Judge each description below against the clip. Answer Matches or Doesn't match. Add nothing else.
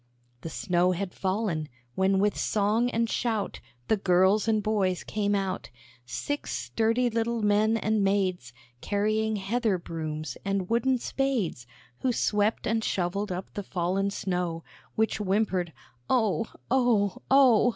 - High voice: Matches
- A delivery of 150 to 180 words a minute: Doesn't match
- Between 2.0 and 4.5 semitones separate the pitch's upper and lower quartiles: Matches